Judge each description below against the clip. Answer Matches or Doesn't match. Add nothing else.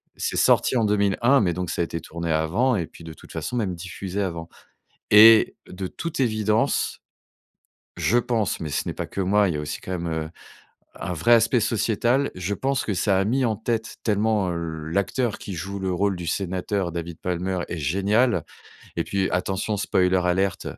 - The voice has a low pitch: Matches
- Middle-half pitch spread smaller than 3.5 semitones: Doesn't match